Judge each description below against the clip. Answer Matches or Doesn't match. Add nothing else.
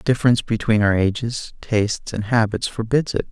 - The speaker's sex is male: Matches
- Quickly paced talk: Doesn't match